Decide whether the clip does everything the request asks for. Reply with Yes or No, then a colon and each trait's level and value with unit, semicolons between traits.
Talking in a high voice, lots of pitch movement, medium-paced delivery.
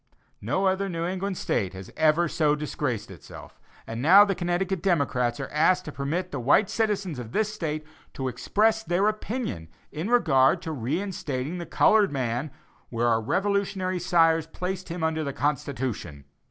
No: medium, 160 Hz; wide, 6.1 semitones; average, 165 wpm